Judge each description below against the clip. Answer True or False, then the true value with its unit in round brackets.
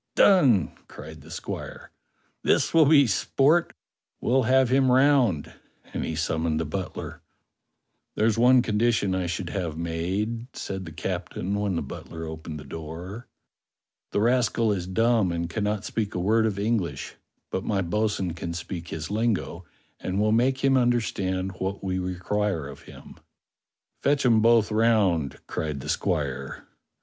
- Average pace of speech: True (155 wpm)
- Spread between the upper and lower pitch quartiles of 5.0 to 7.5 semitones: True (5.4 semitones)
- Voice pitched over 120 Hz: False (100 Hz)